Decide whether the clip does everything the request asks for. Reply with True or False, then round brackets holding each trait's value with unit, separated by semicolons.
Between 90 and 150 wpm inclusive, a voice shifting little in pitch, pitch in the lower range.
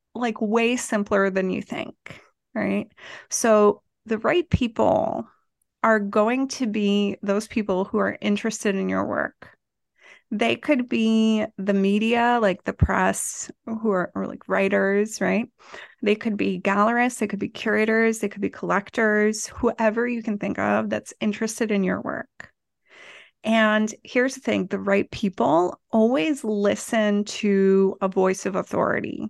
False (145 wpm; 2.3 semitones; 215 Hz)